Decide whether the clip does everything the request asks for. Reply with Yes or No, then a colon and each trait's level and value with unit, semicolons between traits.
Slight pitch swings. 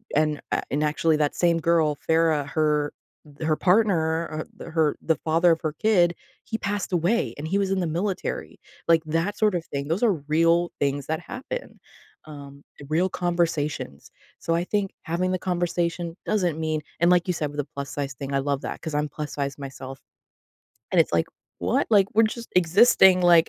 No: average, 3.2 semitones